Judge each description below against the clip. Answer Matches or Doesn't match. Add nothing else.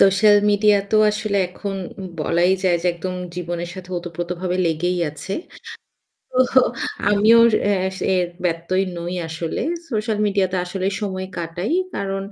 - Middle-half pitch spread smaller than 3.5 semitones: Matches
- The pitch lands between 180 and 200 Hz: Matches